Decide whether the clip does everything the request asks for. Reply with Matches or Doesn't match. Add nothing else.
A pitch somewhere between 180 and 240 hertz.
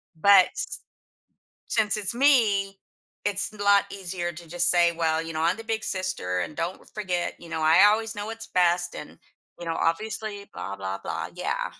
Matches